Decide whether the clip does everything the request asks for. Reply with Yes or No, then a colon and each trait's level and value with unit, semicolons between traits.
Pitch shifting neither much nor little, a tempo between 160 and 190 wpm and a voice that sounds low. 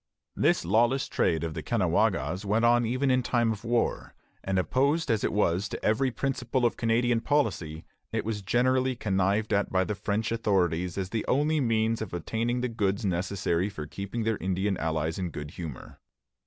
Yes: average, 4.3 semitones; average, 180 wpm; low, 110 Hz